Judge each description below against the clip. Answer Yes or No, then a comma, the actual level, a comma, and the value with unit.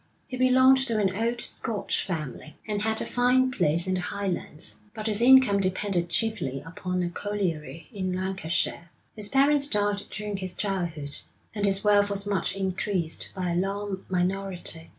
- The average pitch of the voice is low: No, high, 195 Hz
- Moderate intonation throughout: Yes, average, 3.0 semitones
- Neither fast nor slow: Yes, average, 165 wpm